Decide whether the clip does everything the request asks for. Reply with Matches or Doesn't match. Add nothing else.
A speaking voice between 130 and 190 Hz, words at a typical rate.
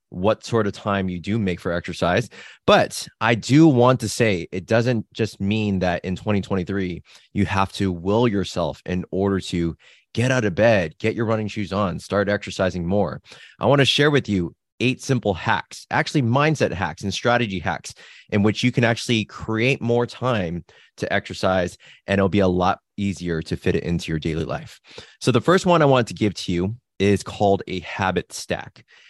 Doesn't match